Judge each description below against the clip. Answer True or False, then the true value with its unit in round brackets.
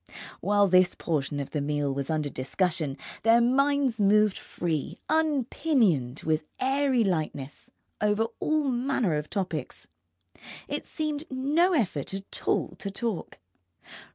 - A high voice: True (205 Hz)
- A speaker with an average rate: False (125 wpm)